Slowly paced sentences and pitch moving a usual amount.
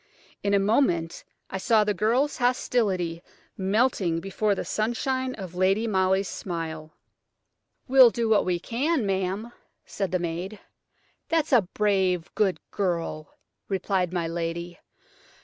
Yes: slow, 130 wpm; average, 4.4 semitones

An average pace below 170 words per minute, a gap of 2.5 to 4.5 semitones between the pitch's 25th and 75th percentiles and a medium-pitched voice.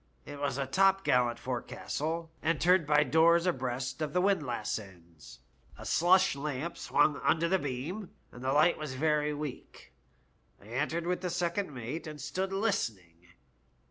No: average, 150 wpm; average, 5.1 semitones; medium, 150 Hz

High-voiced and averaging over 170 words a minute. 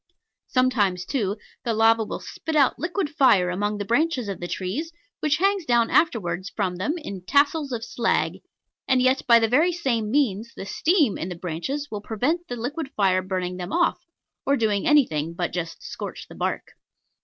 Yes: high, 230 Hz; average, 185 wpm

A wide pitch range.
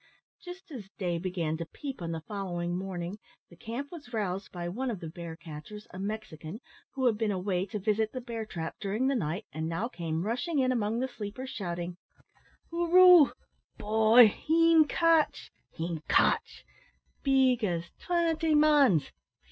Yes: wide, 7.1 semitones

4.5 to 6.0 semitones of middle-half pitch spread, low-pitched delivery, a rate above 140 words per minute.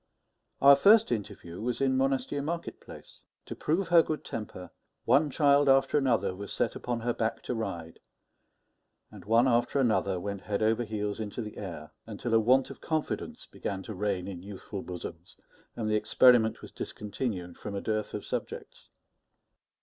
Yes: average, 4.9 semitones; low, 110 Hz; average, 170 wpm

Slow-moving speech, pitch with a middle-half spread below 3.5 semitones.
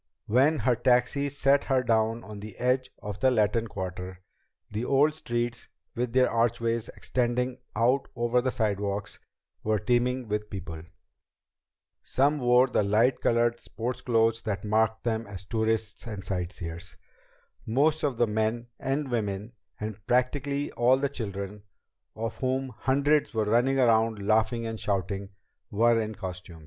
No: average, 150 wpm; average, 3.1 semitones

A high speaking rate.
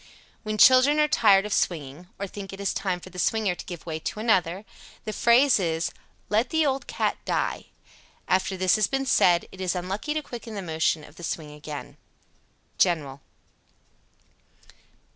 No: average, 175 wpm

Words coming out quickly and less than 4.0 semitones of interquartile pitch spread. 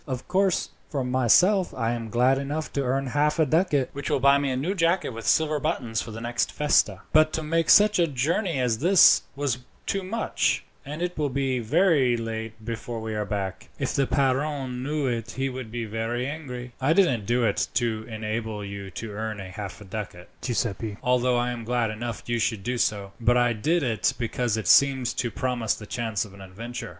No: fast, 210 wpm; average, 4.3 semitones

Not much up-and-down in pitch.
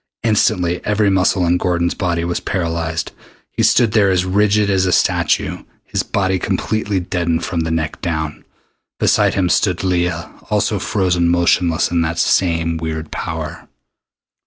Yes: narrow, 2.3 semitones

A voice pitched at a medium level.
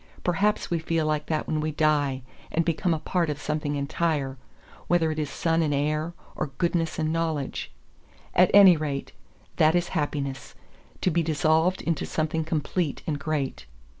Yes: medium, 155 Hz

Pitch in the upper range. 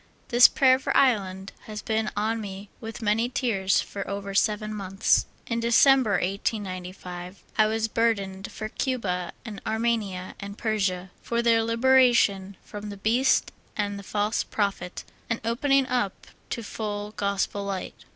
Yes: high, 210 Hz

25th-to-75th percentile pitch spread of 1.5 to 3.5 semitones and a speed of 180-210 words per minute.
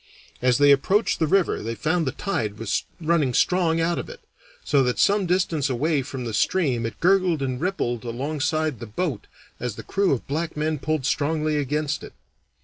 No: average, 4.9 semitones; average, 190 wpm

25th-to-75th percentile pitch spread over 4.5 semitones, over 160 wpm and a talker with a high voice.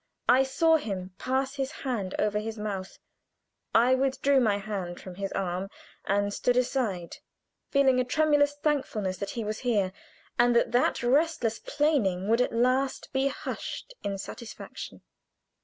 No: average, 5.0 semitones; average, 150 wpm; high, 240 Hz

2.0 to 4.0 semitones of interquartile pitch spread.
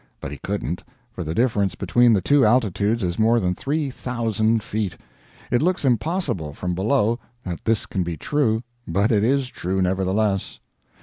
No: average, 4.7 semitones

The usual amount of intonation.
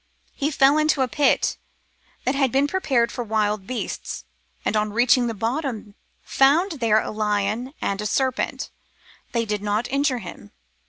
Yes: average, 4.4 semitones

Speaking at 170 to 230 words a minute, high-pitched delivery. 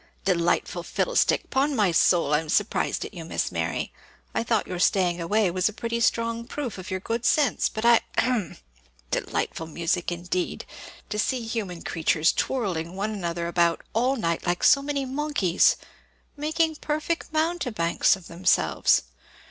No: average, 155 wpm; high, 205 Hz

